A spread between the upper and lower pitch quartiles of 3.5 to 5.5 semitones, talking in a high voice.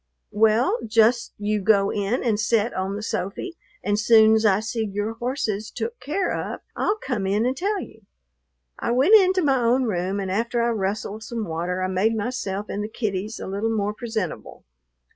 No: average, 2.9 semitones; high, 220 Hz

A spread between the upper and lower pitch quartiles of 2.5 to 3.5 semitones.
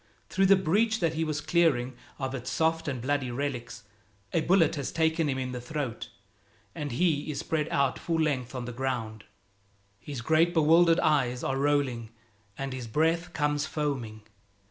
No: average, 4.2 semitones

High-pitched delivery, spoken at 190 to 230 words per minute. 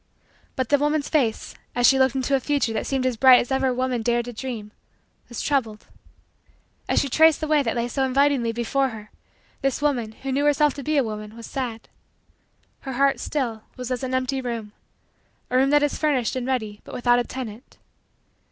Yes: very high, 255 Hz; fast, 205 wpm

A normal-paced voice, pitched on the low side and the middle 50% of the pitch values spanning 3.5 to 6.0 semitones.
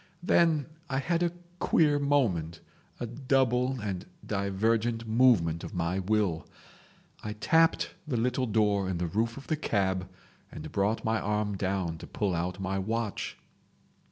Yes: average, 150 wpm; low, 110 Hz; average, 5.1 semitones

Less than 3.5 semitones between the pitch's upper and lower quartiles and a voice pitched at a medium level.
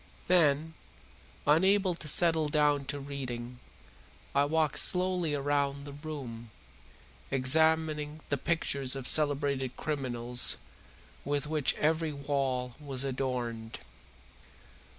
Yes: average, 2.9 semitones; medium, 145 Hz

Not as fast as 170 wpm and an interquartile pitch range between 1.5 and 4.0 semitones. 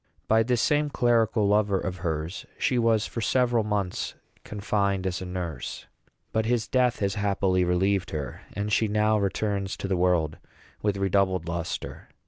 Yes: average, 160 wpm; average, 3.2 semitones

